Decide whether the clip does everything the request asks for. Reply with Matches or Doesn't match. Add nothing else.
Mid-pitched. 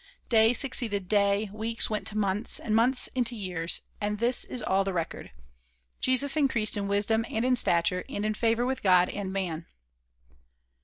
Doesn't match